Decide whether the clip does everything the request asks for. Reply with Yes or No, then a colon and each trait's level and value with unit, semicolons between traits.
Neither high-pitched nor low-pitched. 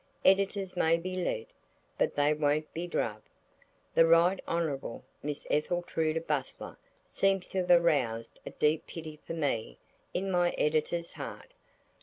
Yes: medium, 165 Hz